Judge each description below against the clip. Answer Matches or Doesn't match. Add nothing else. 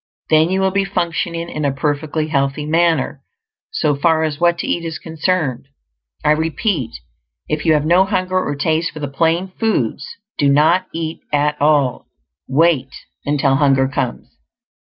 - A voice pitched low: Doesn't match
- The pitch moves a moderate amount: Matches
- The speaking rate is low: Doesn't match